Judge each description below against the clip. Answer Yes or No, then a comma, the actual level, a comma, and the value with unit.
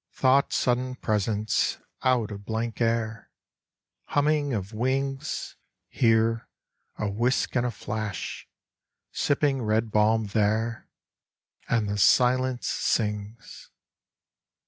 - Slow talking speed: Yes, slow, 100 wpm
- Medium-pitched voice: No, low, 115 Hz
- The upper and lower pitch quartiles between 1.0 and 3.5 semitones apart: Yes, average, 3.0 semitones